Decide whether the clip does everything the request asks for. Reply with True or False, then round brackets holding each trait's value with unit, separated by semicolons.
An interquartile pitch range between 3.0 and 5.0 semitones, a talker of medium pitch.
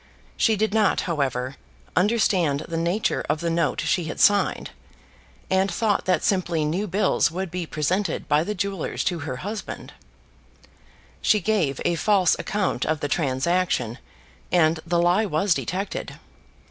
True (4.2 semitones; 175 Hz)